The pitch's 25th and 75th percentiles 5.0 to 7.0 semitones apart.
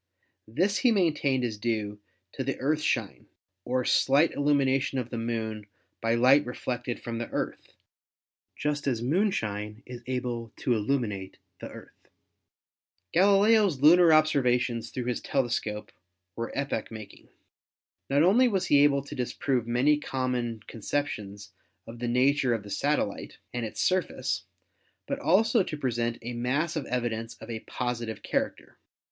No: average, 4.0 semitones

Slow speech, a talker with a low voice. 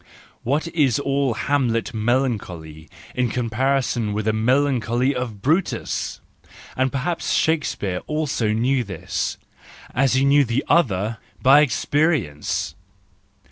Yes: slow, 110 wpm; low, 125 Hz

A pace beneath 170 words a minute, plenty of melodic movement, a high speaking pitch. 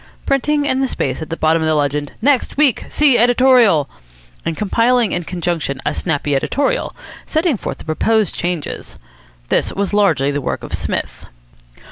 Yes: average, 160 wpm; wide, 8.4 semitones; high, 195 Hz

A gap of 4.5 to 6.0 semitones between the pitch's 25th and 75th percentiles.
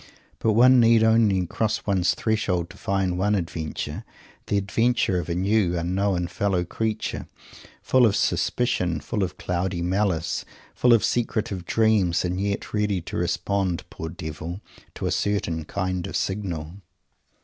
No: average, 3.4 semitones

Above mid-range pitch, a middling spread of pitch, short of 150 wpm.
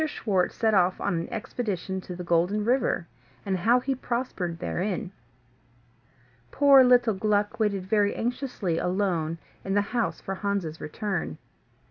Yes: high, 200 Hz; average, 4.3 semitones; average, 140 wpm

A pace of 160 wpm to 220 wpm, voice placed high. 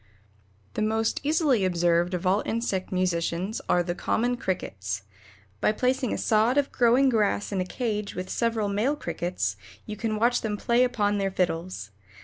Yes: average, 165 wpm; high, 210 Hz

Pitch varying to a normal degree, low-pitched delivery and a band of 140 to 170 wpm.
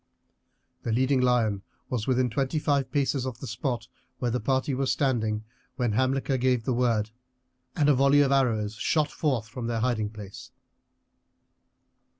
Yes: average, 3.2 semitones; low, 125 Hz; average, 160 wpm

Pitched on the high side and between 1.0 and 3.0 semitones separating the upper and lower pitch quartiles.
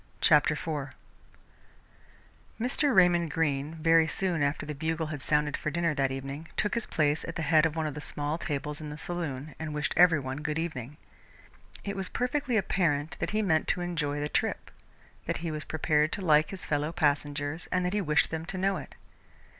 No: medium, 155 Hz; average, 2.7 semitones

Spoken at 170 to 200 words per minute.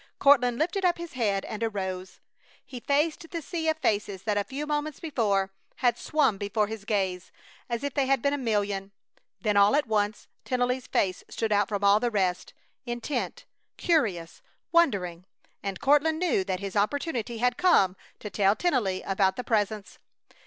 Yes: average, 175 wpm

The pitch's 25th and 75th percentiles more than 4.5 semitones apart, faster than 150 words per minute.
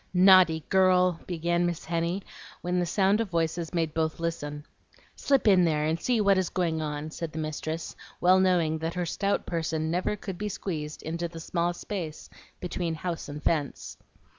No: narrow, 2.5 semitones; average, 180 wpm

